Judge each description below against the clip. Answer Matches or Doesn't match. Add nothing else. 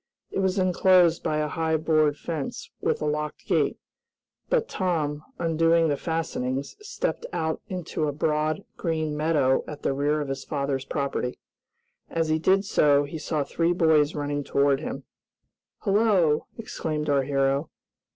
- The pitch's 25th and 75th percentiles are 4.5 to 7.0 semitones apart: Doesn't match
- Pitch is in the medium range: Matches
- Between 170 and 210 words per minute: Doesn't match